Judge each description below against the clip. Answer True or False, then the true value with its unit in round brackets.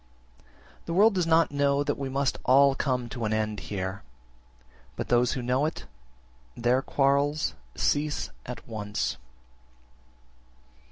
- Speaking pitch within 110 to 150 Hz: True (135 Hz)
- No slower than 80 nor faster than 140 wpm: True (135 wpm)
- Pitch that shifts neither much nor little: True (3.3 semitones)